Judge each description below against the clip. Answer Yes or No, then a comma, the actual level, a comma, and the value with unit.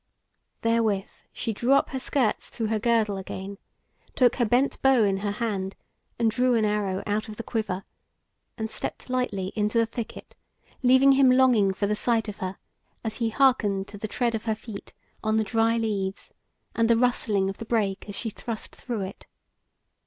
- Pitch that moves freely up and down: No, average, 2.7 semitones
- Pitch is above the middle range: Yes, high, 220 Hz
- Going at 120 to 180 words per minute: No, average, 190 wpm